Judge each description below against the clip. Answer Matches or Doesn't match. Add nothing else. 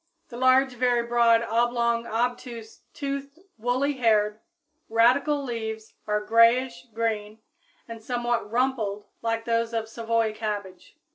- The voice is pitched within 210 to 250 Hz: Matches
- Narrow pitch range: Matches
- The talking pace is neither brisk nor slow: Doesn't match